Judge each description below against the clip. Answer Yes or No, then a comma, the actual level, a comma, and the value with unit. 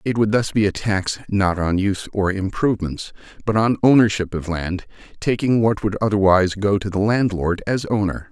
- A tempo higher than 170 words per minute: Yes, average, 190 wpm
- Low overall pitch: Yes, low, 100 Hz